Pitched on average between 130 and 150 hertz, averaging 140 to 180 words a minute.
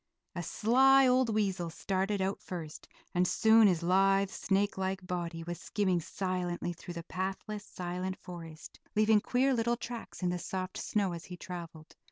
No: high, 190 Hz; average, 165 wpm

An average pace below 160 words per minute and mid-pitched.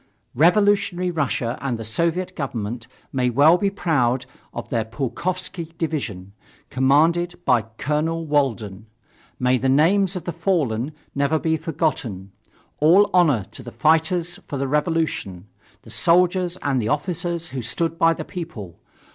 Yes: average, 140 wpm; medium, 155 Hz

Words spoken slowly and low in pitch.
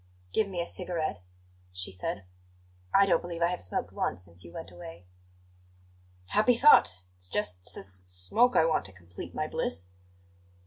No: average, 170 wpm; very low, 95 Hz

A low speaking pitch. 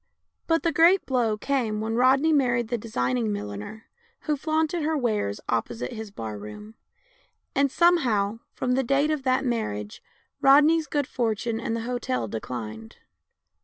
No: high, 235 Hz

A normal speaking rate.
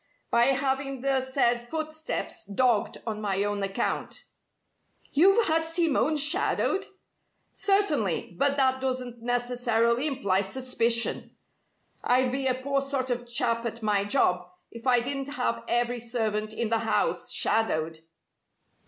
No: slow, 130 wpm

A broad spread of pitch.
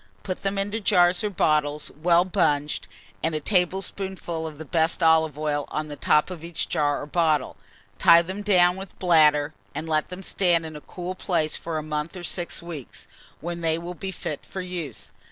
No: average, 2.9 semitones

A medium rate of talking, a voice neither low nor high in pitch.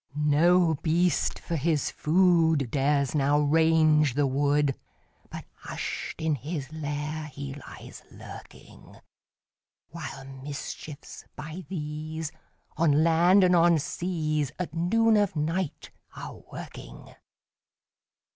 No: slow, 110 wpm; medium, 155 Hz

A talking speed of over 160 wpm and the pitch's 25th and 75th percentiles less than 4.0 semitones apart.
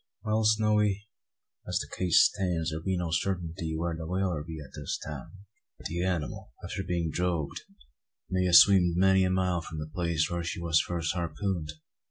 Yes: average, 180 wpm; narrow, 2.6 semitones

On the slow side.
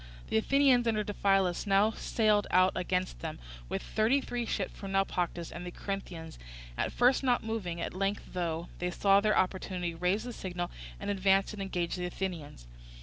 No: average, 175 wpm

